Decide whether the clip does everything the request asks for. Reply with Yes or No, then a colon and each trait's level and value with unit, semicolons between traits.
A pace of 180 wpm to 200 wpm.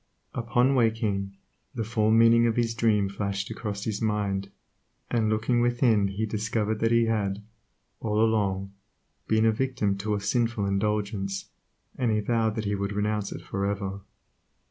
No: average, 160 wpm